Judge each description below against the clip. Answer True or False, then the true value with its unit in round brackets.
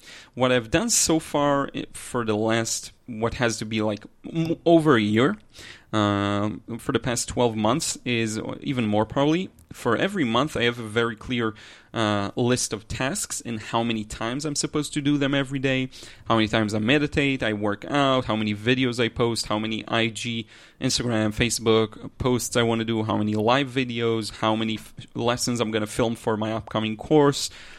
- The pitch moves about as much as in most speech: True (3.0 semitones)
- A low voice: True (115 Hz)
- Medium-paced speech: True (190 wpm)